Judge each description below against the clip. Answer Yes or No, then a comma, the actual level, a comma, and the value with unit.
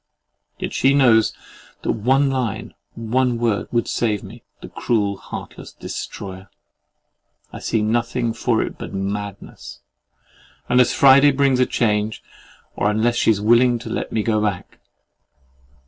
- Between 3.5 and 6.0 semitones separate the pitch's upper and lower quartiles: No, average, 3.0 semitones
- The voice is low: Yes, low, 115 Hz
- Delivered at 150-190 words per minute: No, average, 140 wpm